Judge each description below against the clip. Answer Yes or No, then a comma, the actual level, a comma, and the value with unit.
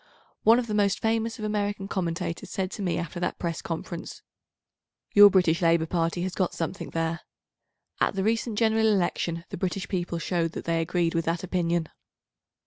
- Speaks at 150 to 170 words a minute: No, average, 180 wpm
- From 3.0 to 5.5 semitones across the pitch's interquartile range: Yes, average, 3.4 semitones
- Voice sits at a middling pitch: Yes, medium, 180 Hz